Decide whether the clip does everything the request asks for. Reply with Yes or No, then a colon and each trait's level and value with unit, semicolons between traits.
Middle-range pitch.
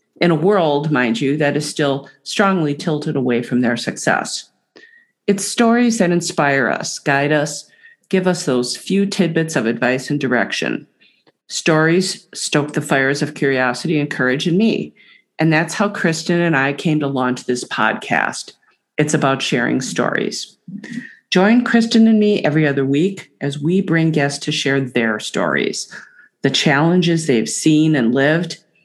Yes: medium, 155 Hz